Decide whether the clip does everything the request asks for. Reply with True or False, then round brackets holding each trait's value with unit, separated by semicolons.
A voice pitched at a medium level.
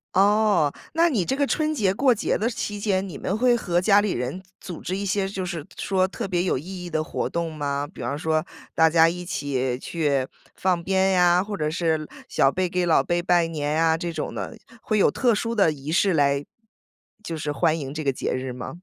True (175 Hz)